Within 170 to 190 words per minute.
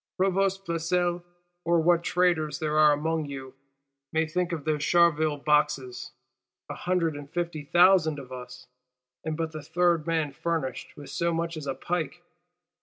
No: average, 160 wpm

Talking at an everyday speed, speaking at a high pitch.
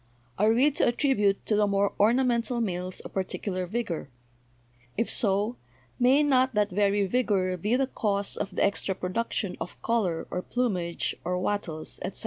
Yes: average, 165 wpm; high, 205 Hz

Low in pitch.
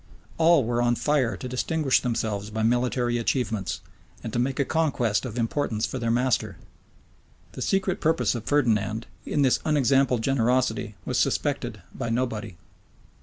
Yes: low, 125 Hz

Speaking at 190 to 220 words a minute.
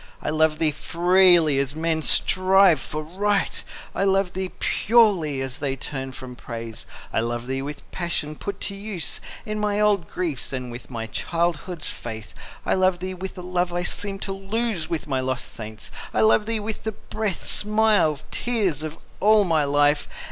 No: average, 180 wpm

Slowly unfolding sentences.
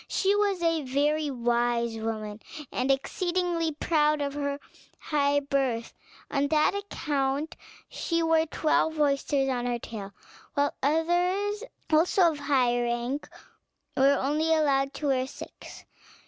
Yes: slow, 130 wpm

